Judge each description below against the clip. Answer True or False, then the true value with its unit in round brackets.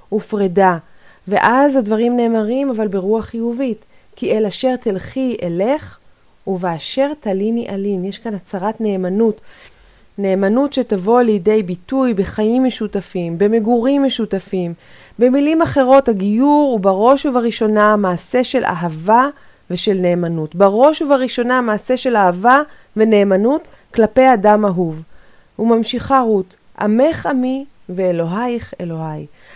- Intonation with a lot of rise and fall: False (4.6 semitones)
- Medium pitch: False (220 Hz)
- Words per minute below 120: True (110 wpm)